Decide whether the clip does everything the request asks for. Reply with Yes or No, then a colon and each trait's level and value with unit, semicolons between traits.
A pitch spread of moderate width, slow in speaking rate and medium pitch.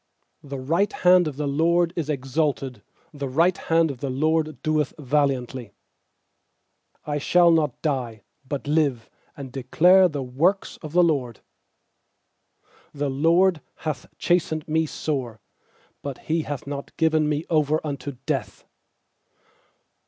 Yes: average, 3.1 semitones; slow, 130 wpm; medium, 150 Hz